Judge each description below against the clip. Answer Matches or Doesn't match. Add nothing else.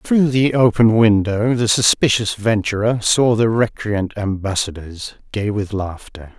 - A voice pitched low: Matches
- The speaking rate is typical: Doesn't match